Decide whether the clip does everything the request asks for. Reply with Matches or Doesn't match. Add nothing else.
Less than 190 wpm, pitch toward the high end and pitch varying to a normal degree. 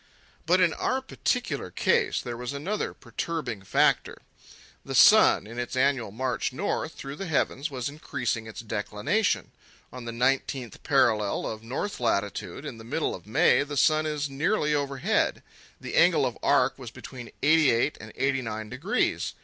Doesn't match